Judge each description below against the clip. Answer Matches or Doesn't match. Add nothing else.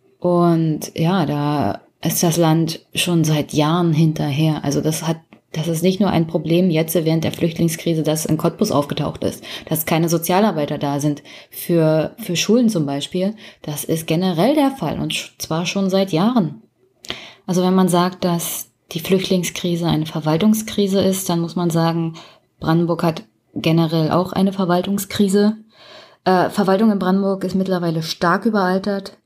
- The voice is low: Doesn't match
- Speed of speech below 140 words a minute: Doesn't match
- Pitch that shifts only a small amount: Doesn't match